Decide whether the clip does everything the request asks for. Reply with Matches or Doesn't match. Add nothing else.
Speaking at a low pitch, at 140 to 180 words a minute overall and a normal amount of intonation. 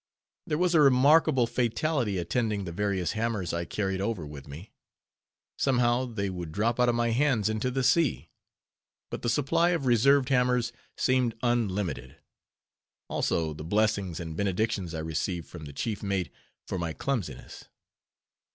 Doesn't match